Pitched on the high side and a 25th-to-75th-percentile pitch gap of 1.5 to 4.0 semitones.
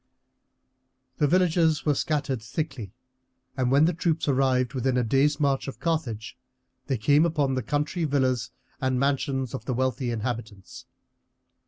No: low, 135 Hz; average, 2.8 semitones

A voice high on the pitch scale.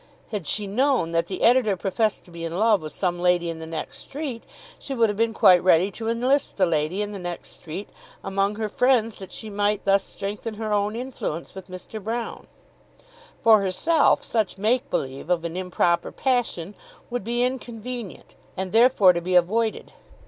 Yes: high, 205 Hz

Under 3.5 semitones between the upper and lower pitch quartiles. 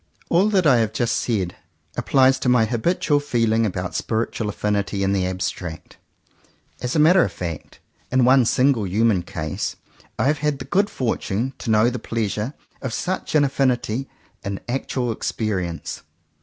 No: average, 4.8 semitones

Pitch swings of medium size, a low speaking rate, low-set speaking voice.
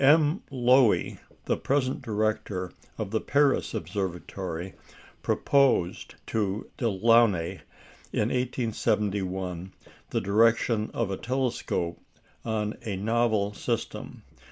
Yes: average, 3.9 semitones; slow, 95 wpm; low, 110 Hz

